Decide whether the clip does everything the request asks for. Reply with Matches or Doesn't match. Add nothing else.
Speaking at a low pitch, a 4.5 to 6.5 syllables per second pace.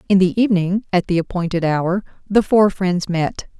Doesn't match